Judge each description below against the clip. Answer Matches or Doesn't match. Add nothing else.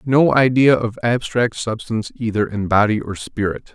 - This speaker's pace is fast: Doesn't match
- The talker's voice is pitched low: Matches